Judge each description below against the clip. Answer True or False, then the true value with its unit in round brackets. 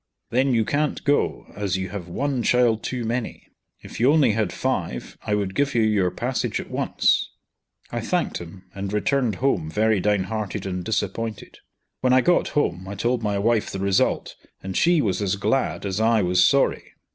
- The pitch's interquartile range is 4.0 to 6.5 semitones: True (4.3 semitones)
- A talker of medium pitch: False (110 Hz)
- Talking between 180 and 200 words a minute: True (185 wpm)